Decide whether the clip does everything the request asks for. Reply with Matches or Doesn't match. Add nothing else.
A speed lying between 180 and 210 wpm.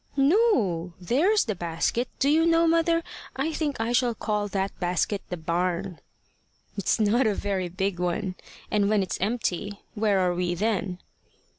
Doesn't match